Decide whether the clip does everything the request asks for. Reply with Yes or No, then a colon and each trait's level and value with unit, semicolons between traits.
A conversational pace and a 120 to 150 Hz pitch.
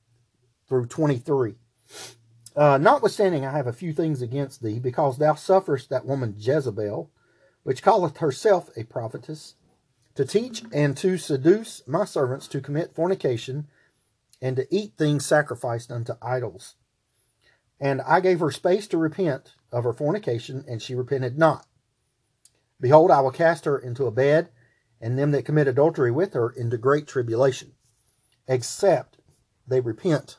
Yes: average, 145 wpm; low, 135 Hz